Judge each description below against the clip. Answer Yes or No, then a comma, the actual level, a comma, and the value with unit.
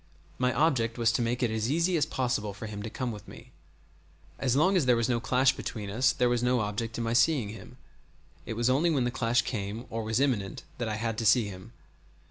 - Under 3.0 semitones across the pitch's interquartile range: Yes, narrow, 2.6 semitones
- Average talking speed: No, fast, 240 wpm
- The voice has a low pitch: Yes, low, 120 Hz